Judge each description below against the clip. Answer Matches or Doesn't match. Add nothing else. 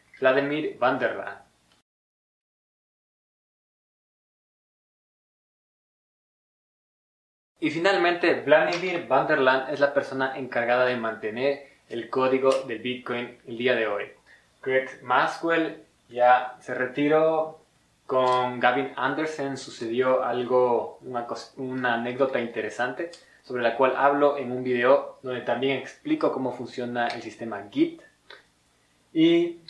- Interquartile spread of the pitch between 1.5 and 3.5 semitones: Matches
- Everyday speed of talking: Doesn't match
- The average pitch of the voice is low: Matches